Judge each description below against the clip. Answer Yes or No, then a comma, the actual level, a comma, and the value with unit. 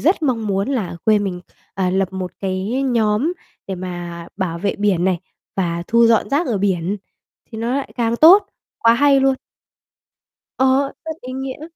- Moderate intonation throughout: No, wide, 6.0 semitones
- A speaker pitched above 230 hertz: No, high, 215 Hz